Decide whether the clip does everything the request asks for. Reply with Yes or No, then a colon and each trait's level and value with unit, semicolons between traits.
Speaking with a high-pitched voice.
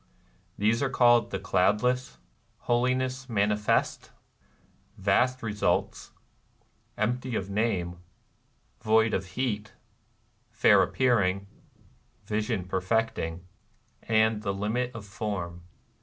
No: low, 110 Hz